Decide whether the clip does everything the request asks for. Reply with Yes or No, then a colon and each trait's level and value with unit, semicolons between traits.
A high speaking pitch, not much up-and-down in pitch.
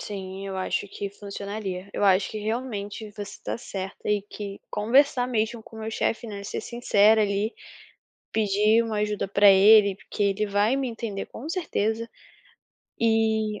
Yes: high, 210 Hz; narrow, 1.9 semitones